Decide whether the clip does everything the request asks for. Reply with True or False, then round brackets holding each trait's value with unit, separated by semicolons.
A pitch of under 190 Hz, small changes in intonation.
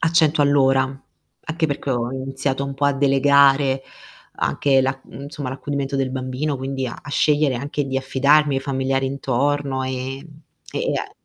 True (135 Hz; 1.3 semitones)